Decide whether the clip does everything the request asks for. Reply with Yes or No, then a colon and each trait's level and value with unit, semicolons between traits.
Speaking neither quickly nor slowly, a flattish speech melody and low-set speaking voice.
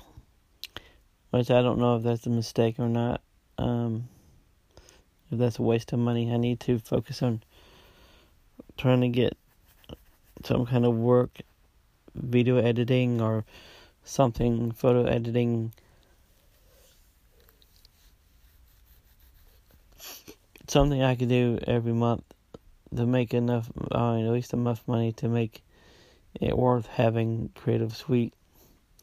No: slow, 115 wpm; narrow, 1.4 semitones; low, 120 Hz